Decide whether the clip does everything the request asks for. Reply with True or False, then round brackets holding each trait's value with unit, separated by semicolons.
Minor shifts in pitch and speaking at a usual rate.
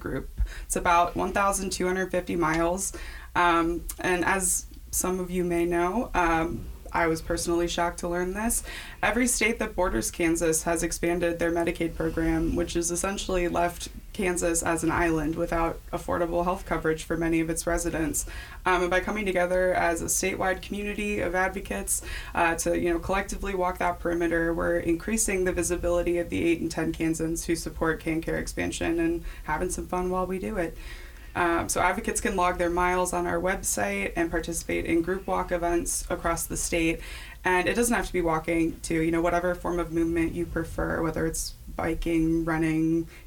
True (1.7 semitones; 180 wpm)